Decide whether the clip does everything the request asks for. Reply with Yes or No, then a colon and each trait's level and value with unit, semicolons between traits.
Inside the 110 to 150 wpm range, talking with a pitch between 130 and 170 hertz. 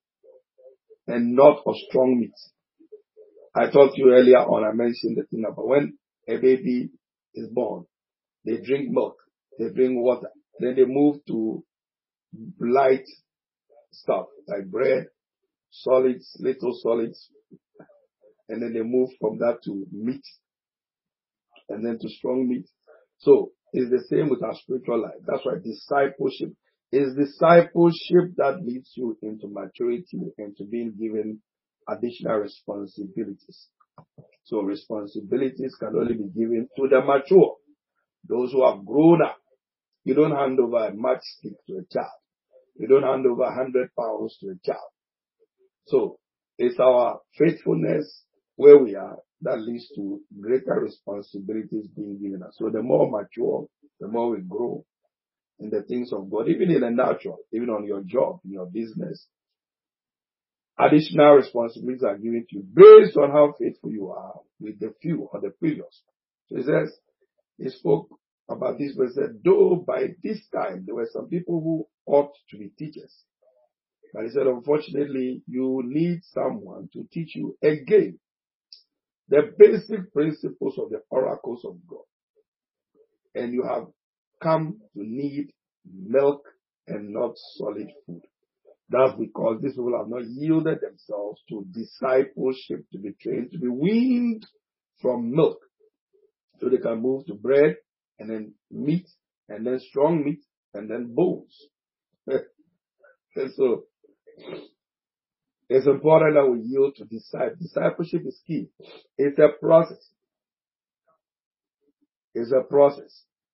Yes: average, 140 wpm; medium, 140 Hz